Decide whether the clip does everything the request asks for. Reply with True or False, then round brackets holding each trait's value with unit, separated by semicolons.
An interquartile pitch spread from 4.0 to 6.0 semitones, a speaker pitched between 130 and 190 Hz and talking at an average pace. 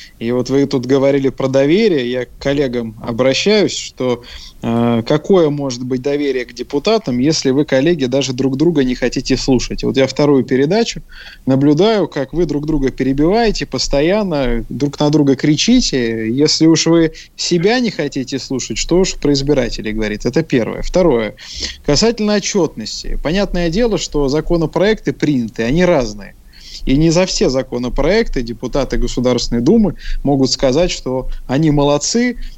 True (4.3 semitones; 140 Hz; 145 wpm)